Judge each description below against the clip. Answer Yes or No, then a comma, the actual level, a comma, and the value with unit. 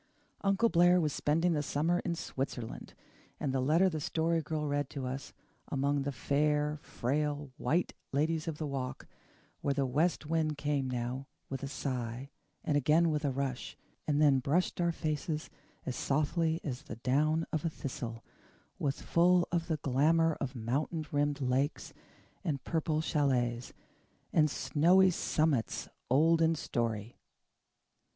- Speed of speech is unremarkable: Yes, average, 150 wpm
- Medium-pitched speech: Yes, medium, 150 Hz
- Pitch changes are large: No, average, 3.1 semitones